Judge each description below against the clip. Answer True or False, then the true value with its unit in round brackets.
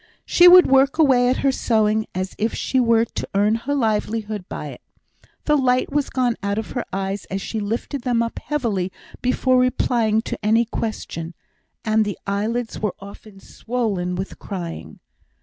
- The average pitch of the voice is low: False (225 Hz)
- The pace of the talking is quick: False (170 wpm)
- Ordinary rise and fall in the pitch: True (3.7 semitones)